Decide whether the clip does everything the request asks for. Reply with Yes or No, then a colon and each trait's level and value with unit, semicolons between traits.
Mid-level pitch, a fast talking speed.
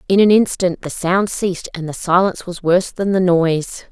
Yes: medium, 180 Hz; fast, 215 wpm